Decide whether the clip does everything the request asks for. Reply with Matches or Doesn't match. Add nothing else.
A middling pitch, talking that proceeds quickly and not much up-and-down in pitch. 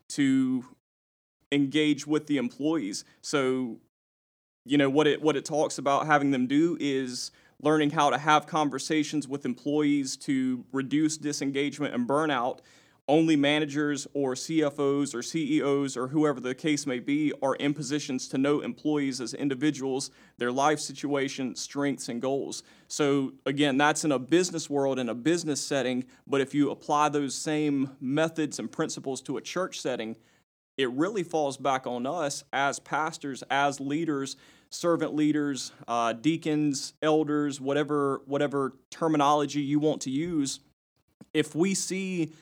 Doesn't match